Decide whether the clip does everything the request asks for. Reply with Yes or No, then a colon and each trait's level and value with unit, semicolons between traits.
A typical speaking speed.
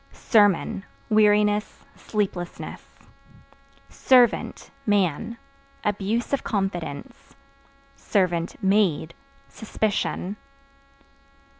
No: slow, 50 wpm